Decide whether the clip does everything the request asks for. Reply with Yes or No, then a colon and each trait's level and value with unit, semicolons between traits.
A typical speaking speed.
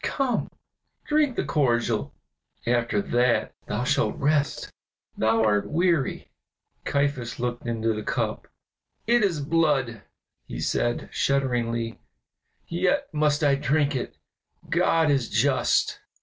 No: slow, 115 wpm